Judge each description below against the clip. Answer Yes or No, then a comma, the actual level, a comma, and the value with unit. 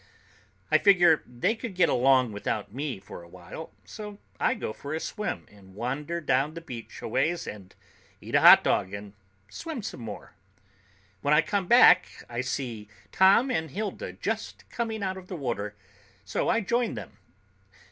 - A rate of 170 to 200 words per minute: Yes, average, 175 wpm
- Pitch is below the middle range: No, medium, 150 Hz